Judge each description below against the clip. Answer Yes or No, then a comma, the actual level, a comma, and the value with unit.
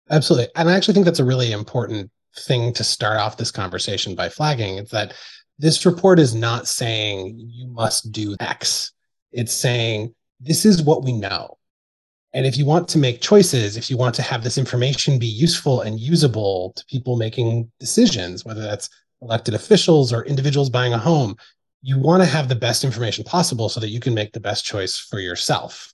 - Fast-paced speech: No, average, 195 wpm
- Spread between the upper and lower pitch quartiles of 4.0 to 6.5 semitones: Yes, average, 4.8 semitones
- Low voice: Yes, low, 120 Hz